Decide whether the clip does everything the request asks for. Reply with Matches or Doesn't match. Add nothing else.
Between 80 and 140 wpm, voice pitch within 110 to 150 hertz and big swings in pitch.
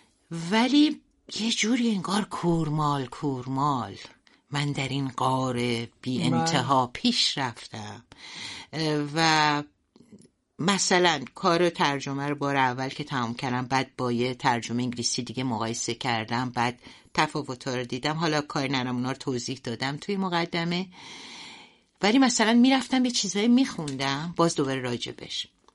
Matches